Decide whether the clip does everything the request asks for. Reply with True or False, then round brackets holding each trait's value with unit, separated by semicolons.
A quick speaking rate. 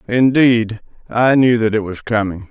False (170 wpm)